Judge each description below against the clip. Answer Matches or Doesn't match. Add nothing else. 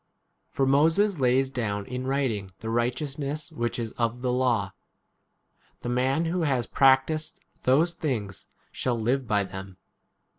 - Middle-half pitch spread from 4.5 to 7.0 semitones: Doesn't match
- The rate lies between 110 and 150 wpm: Matches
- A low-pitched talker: Matches